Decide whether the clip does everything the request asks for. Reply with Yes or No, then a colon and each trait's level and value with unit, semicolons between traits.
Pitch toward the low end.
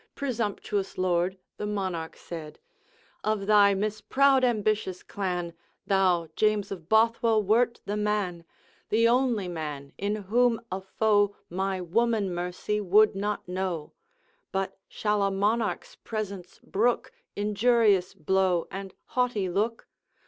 No: high, 200 Hz